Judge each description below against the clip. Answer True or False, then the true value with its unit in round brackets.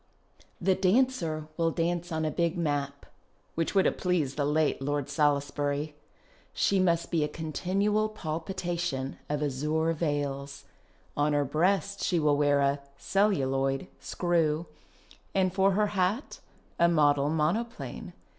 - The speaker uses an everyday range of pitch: True (4.0 semitones)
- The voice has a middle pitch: True (160 Hz)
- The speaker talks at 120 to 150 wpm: True (135 wpm)